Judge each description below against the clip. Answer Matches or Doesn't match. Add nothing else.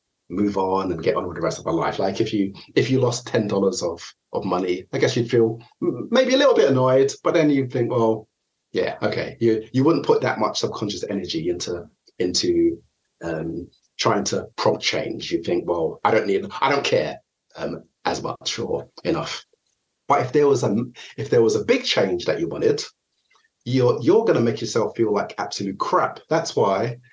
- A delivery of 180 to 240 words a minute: Matches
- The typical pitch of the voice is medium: Doesn't match